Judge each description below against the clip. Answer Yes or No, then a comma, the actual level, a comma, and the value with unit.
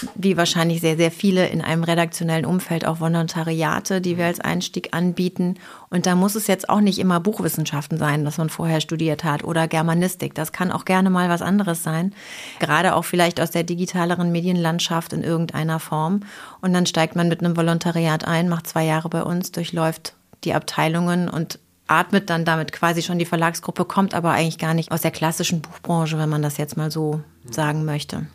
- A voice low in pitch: No, medium, 165 Hz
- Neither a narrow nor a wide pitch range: No, narrow, 1.8 semitones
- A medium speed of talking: No, fast, 195 wpm